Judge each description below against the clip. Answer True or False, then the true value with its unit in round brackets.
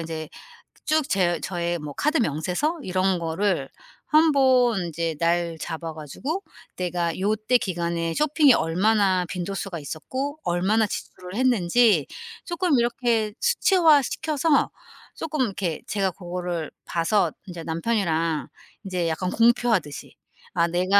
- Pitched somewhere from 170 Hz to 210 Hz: True (190 Hz)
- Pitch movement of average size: False (6.4 semitones)